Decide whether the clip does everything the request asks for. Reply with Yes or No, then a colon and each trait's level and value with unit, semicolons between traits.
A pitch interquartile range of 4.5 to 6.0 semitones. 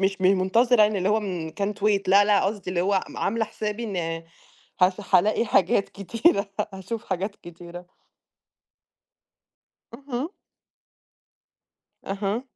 No: average, 2.7 semitones